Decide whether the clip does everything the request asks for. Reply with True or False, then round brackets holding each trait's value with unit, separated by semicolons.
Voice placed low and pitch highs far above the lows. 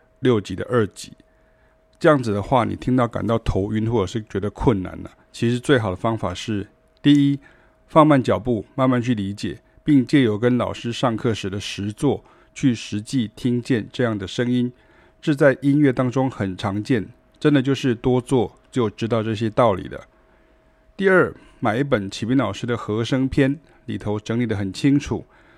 False (120 Hz; 4.1 semitones)